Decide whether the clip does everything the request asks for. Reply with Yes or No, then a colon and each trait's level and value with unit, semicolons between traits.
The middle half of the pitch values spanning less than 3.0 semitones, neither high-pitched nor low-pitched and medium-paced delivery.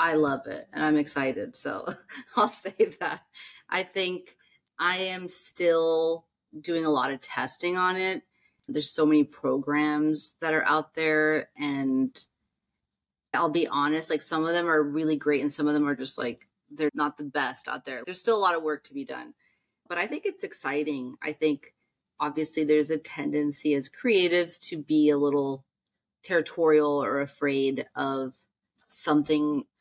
Yes: narrow, 2.4 semitones; medium, 150 Hz; average, 170 wpm